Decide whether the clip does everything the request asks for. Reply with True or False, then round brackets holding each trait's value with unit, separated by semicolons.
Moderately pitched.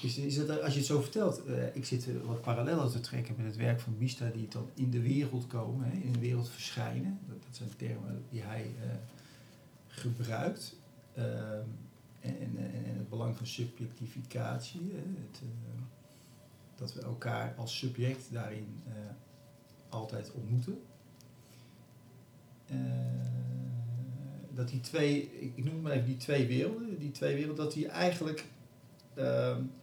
False (125 Hz)